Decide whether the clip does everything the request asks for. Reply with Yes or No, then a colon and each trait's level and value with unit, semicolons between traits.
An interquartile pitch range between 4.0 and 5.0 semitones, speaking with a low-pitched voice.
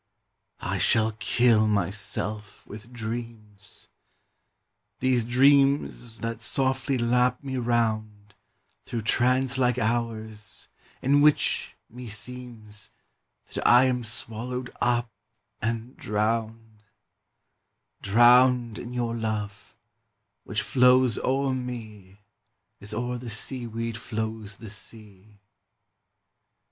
No: narrow, 2.5 semitones; low, 115 Hz